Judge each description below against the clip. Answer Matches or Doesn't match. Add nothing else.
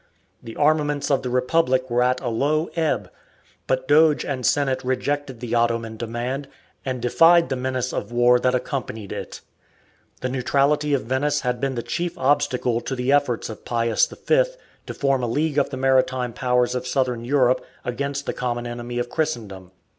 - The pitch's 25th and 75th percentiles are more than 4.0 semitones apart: Doesn't match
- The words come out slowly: Doesn't match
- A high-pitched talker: Doesn't match